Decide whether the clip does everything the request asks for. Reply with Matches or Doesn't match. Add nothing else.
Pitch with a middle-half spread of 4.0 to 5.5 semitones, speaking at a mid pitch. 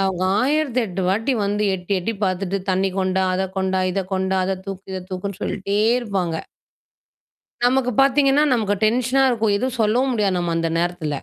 Doesn't match